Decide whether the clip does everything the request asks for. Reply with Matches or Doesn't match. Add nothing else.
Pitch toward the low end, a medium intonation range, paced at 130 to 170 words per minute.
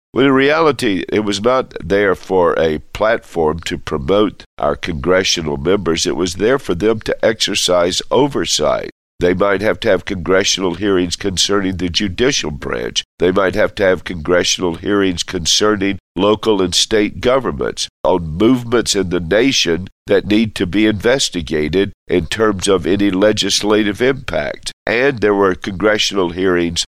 Matches